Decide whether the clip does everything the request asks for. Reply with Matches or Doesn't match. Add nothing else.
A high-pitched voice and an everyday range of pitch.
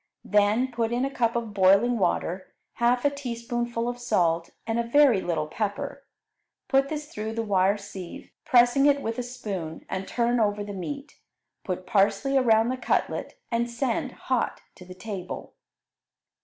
Matches